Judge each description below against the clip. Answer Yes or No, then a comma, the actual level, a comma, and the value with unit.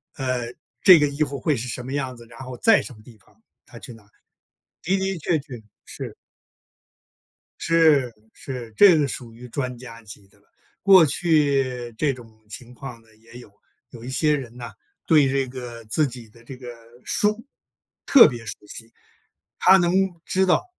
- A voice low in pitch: Yes, low, 130 Hz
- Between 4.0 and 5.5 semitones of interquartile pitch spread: Yes, average, 4.3 semitones